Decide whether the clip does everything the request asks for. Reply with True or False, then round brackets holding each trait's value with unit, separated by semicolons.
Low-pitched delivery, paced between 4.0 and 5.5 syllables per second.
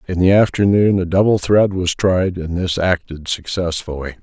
True (90 Hz; 4.8 syllables/s)